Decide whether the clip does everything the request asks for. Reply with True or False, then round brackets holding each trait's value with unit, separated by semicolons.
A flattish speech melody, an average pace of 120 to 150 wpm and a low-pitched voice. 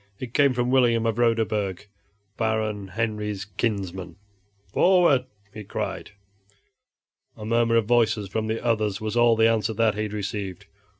True (2.0 semitones; 140 wpm; 110 Hz)